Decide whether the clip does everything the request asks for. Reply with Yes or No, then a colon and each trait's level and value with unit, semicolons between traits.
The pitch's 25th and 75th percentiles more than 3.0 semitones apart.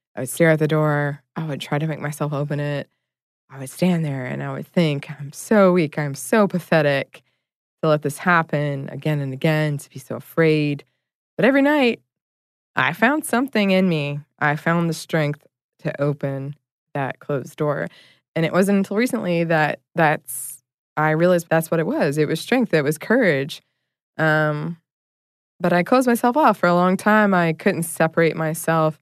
Yes: average, 3.6 semitones